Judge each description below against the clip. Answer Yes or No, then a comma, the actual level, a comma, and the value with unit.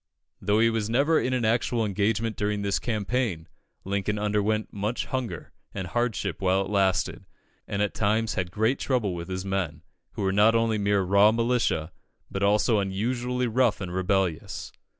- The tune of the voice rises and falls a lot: No, average, 2.9 semitones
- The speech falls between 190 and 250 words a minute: No, average, 170 wpm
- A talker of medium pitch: No, low, 105 Hz